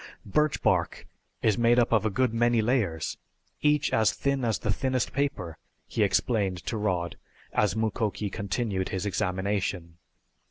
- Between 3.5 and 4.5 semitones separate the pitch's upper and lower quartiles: Yes, average, 4.0 semitones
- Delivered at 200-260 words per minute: No, average, 150 wpm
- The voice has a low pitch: Yes, low, 110 Hz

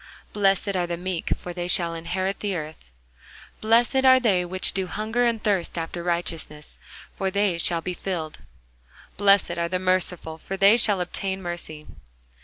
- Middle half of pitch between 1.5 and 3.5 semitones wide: Yes, average, 2.7 semitones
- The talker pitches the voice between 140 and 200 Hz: Yes, medium, 185 Hz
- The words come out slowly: No, average, 165 wpm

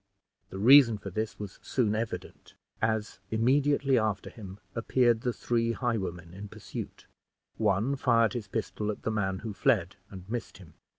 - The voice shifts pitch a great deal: No, average, 3.0 semitones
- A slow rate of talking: No, average, 160 wpm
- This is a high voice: No, low, 110 Hz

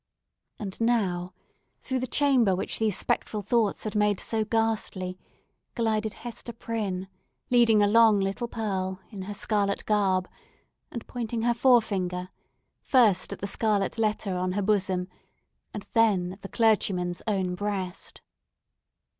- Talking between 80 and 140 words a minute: Yes, slow, 135 wpm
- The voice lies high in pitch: Yes, high, 210 Hz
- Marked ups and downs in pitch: No, average, 3.1 semitones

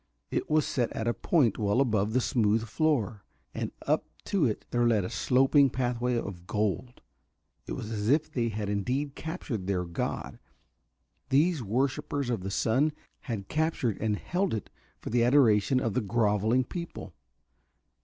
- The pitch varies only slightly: No, average, 4.6 semitones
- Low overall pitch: Yes, low, 120 Hz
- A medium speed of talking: Yes, average, 165 wpm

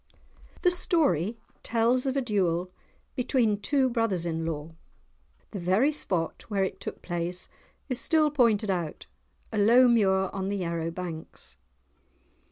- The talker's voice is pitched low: No, high, 200 Hz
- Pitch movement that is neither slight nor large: No, wide, 5.9 semitones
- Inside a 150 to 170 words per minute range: No, average, 140 wpm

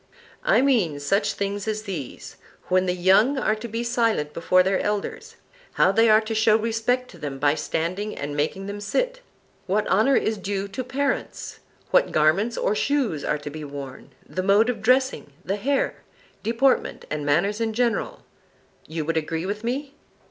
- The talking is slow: No, average, 175 wpm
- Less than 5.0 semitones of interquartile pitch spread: No, wide, 5.6 semitones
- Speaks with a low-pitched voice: No, high, 205 Hz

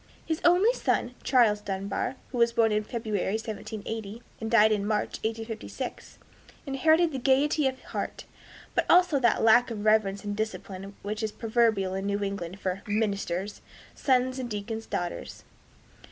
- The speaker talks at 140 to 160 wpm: Yes, average, 155 wpm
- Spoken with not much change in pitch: No, average, 3.4 semitones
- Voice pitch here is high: Yes, high, 220 Hz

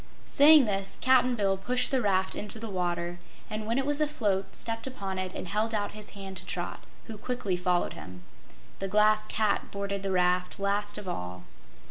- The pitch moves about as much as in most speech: Yes, average, 3.3 semitones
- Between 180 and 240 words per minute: Yes, average, 190 wpm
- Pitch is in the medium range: No, high, 205 Hz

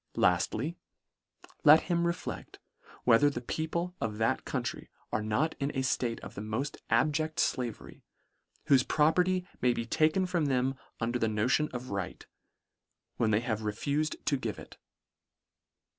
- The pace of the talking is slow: No, average, 155 wpm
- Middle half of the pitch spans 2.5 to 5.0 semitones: No, wide, 5.5 semitones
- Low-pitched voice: Yes, low, 130 Hz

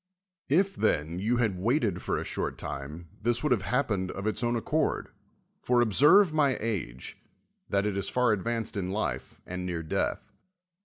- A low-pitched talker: Yes, low, 110 Hz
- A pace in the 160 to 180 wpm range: Yes, average, 170 wpm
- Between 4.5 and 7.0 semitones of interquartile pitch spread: Yes, average, 5.2 semitones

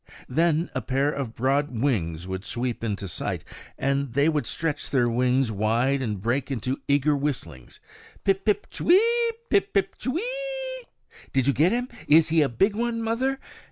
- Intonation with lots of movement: Yes, wide, 8.4 semitones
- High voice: No, medium, 140 Hz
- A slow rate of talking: No, average, 160 wpm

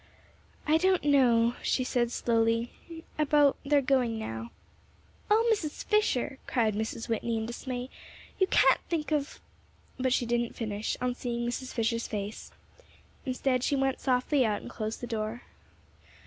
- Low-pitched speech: No, high, 245 Hz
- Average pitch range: Yes, average, 3.4 semitones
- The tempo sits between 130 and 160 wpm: Yes, average, 150 wpm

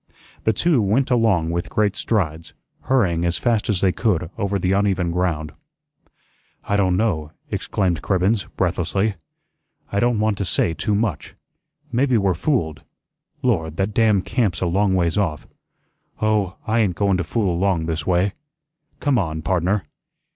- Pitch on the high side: No, very low, 95 Hz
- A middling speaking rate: Yes, average, 155 wpm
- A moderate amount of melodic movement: Yes, average, 3.8 semitones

